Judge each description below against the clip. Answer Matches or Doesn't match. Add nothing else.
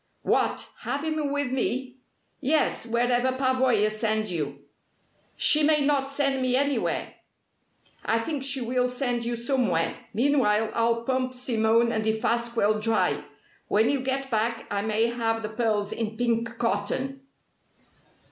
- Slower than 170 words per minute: Matches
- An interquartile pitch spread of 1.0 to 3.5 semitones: Matches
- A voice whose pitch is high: Matches